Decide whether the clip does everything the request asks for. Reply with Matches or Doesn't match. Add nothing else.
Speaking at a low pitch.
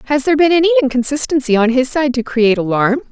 Doesn't match